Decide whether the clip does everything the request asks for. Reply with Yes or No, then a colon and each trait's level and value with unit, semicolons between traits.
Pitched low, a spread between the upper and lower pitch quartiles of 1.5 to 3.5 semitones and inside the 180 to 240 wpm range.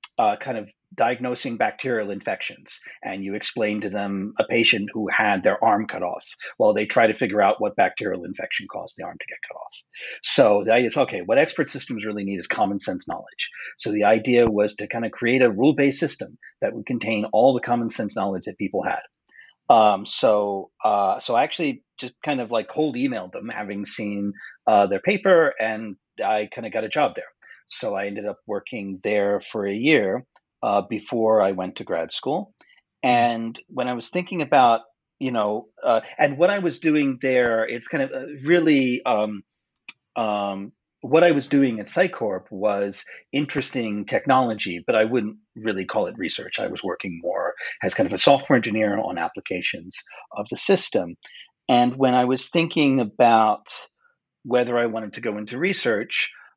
No: low, 115 Hz; average, 3.9 semitones; average, 190 wpm